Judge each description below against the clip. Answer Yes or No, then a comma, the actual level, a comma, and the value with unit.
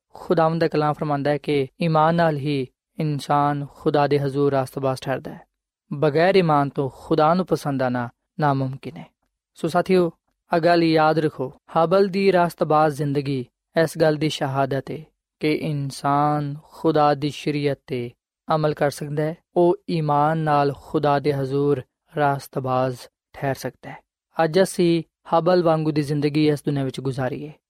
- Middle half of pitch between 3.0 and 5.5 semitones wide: No, narrow, 2.5 semitones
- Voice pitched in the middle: Yes, medium, 150 Hz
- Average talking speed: Yes, average, 150 wpm